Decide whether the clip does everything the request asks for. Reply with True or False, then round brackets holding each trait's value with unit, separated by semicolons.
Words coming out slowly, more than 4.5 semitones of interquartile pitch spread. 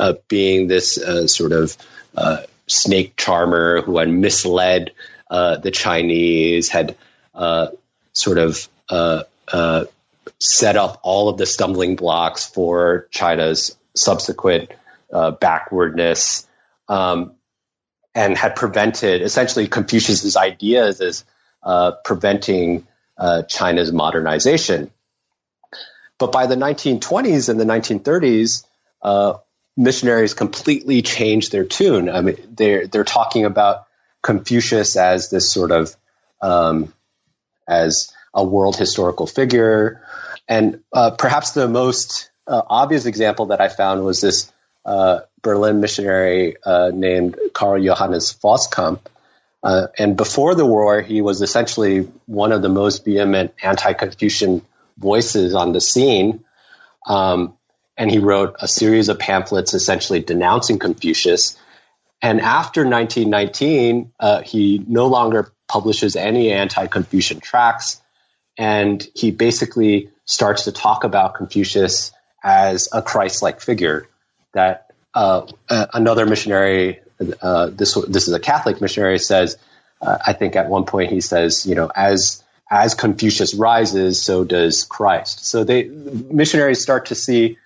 False (130 wpm; 3.6 semitones)